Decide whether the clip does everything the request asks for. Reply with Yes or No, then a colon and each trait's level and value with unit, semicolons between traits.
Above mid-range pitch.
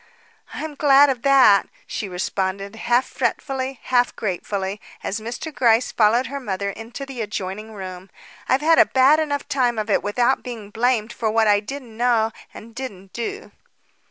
Yes: high, 230 Hz